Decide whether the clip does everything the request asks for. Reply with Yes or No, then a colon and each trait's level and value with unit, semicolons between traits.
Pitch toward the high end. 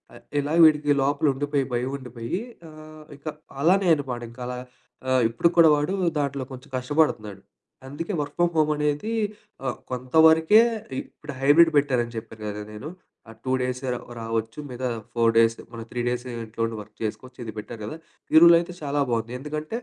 No: low, 135 Hz